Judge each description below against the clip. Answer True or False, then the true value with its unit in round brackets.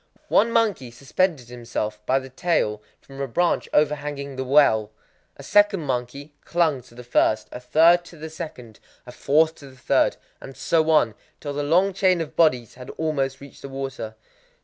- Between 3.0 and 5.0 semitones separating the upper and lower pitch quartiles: True (4.4 semitones)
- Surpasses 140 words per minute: True (175 wpm)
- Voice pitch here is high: False (140 Hz)